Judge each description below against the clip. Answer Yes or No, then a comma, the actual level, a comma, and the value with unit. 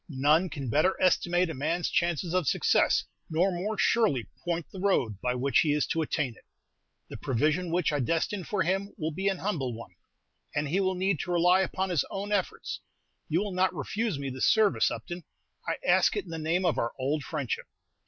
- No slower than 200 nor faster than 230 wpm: Yes, fast, 205 wpm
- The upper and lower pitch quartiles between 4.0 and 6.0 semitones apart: Yes, average, 4.4 semitones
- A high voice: No, medium, 170 Hz